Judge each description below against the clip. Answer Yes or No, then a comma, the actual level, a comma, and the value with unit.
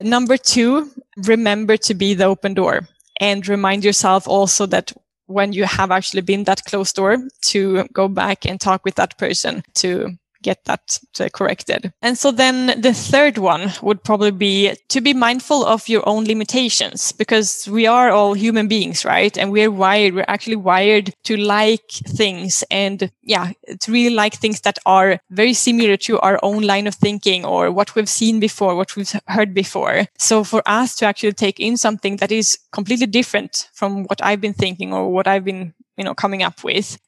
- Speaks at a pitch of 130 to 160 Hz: No, high, 205 Hz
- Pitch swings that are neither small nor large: No, narrow, 2.2 semitones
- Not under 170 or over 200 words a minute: Yes, average, 190 wpm